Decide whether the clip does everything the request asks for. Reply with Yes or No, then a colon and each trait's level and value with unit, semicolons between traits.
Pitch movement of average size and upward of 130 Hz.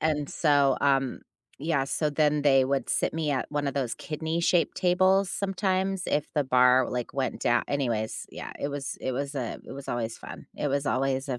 Yes: average, 3.0 semitones; medium, 140 Hz